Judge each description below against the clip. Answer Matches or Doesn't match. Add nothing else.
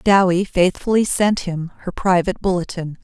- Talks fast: Doesn't match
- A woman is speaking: Matches